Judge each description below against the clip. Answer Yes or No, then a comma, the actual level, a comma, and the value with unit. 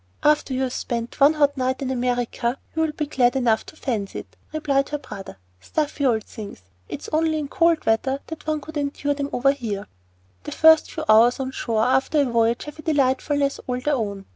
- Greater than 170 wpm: Yes, average, 200 wpm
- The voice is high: Yes, very high, 270 Hz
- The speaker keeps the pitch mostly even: No, average, 3.7 semitones